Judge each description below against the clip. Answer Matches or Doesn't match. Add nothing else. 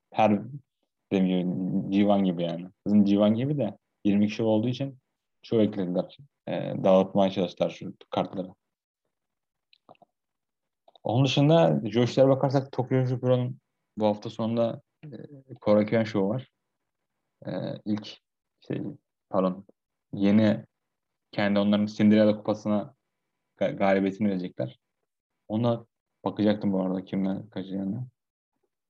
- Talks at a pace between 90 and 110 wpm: Matches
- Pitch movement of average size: Matches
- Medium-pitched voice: Doesn't match